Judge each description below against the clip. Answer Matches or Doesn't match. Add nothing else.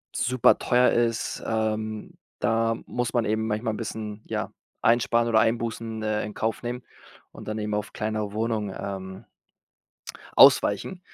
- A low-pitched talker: Matches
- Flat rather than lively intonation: Matches